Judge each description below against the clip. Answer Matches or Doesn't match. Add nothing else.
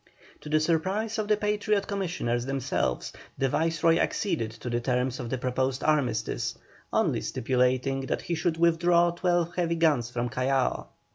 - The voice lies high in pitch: Doesn't match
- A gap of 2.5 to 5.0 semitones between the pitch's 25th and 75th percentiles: Doesn't match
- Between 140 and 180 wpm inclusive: Matches